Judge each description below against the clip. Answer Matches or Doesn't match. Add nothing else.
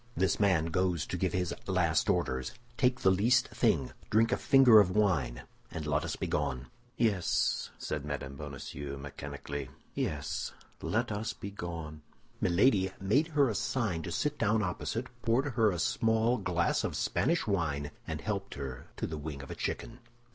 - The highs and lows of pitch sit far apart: Matches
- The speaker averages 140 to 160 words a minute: Doesn't match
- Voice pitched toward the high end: Doesn't match